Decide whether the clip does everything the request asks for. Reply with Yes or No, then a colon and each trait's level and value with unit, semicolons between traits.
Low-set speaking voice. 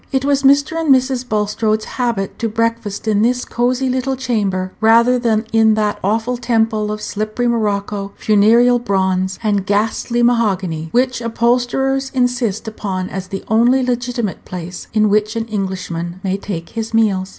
No: high, 225 Hz